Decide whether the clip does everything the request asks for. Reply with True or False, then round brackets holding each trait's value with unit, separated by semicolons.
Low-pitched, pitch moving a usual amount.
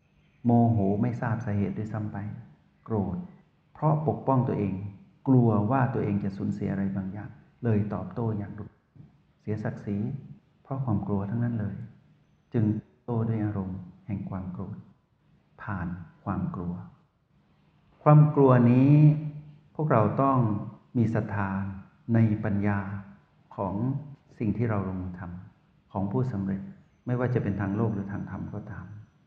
True (110 Hz; 4.0 semitones)